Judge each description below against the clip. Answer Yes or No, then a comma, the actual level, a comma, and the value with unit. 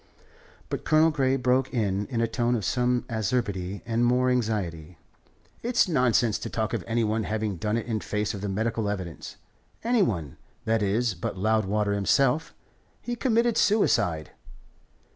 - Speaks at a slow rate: No, average, 160 wpm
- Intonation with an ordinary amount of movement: Yes, average, 3.7 semitones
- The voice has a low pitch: Yes, low, 115 Hz